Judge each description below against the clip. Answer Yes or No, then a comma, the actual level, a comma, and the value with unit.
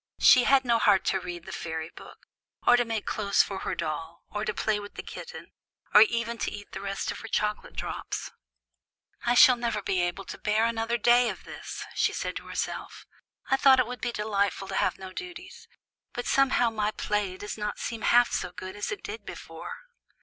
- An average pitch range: Yes, average, 3.6 semitones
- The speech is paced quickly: Yes, fast, 215 wpm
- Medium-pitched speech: No, high, 215 Hz